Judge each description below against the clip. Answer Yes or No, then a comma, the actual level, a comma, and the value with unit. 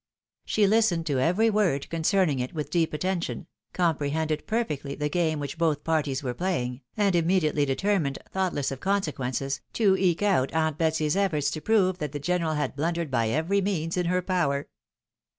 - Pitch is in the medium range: Yes, medium, 160 Hz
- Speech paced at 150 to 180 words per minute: Yes, average, 170 wpm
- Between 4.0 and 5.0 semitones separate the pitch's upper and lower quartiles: Yes, average, 4.3 semitones